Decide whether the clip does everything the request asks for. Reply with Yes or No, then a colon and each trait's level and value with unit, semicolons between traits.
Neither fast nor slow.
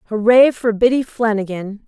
No: slow, 130 wpm